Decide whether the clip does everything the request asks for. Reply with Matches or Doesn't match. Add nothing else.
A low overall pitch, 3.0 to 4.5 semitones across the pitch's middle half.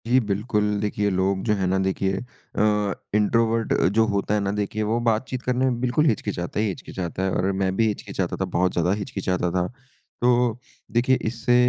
Matches